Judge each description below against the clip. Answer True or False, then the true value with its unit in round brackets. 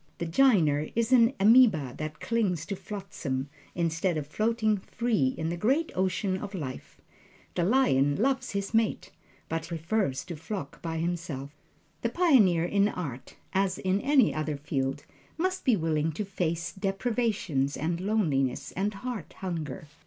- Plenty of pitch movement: True (5.8 semitones)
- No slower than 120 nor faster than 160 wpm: True (150 wpm)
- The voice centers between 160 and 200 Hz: True (185 Hz)